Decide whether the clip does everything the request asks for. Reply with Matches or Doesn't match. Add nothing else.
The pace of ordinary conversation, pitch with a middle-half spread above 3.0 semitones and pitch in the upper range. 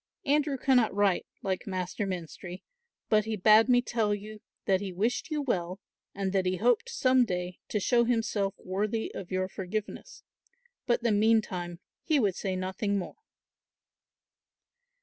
Matches